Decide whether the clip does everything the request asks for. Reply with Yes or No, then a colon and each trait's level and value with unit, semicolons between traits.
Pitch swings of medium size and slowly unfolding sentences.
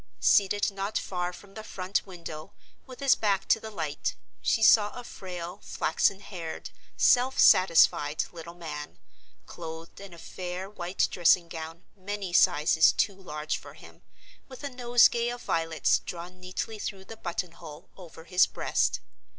No: average, 3.6 semitones; average, 155 wpm